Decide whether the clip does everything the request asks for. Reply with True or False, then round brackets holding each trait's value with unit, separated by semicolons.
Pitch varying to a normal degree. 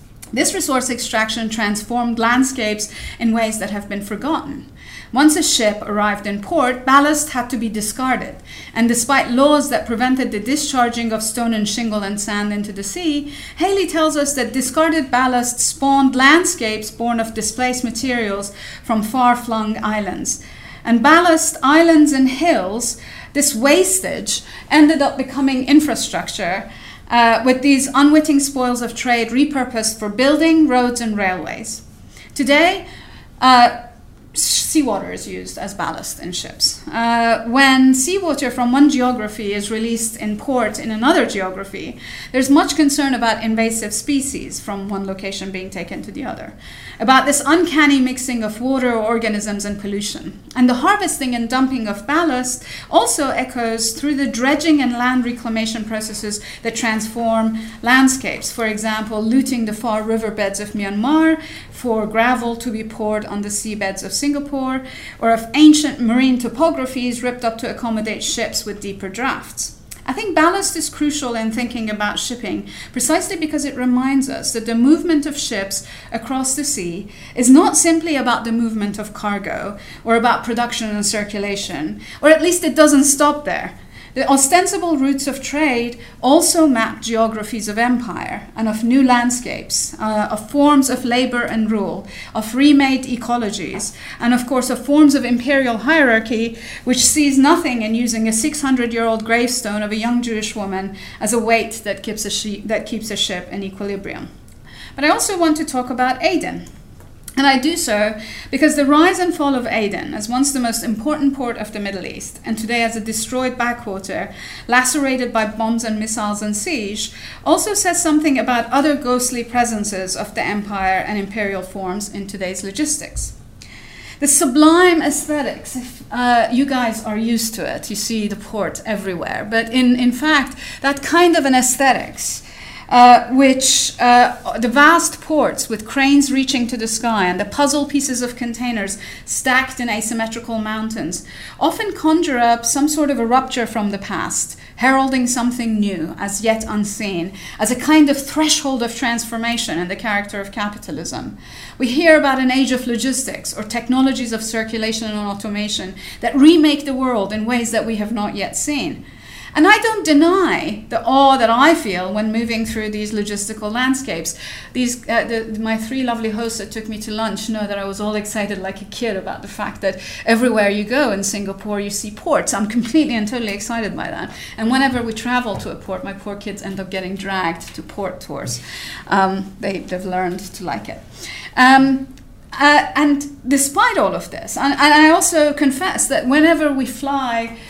True (4.3 semitones)